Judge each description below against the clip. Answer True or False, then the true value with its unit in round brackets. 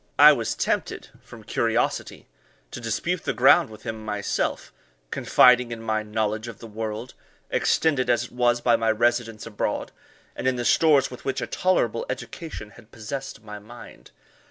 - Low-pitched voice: True (115 Hz)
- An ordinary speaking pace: True (165 wpm)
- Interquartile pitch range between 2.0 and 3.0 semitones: True (2.5 semitones)